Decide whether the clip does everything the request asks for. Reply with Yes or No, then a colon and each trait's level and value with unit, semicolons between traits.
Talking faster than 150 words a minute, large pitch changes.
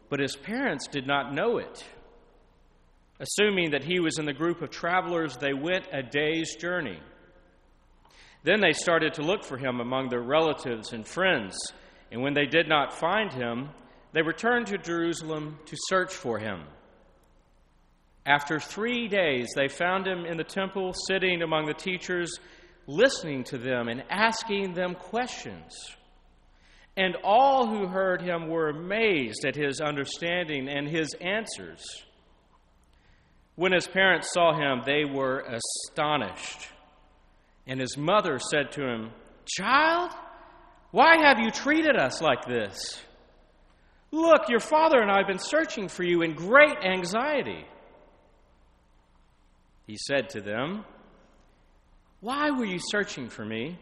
No: average, 140 wpm; wide, 6.2 semitones